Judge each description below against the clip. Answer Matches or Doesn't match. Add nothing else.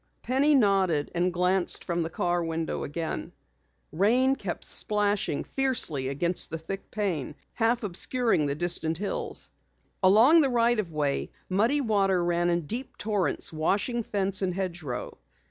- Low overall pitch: Doesn't match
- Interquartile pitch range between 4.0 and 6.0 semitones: Matches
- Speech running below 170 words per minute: Matches